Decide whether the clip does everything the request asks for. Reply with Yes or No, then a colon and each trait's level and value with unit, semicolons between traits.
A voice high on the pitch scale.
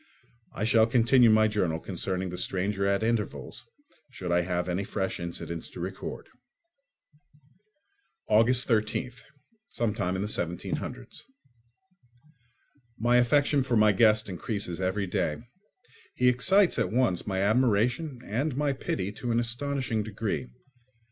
No: low, 110 Hz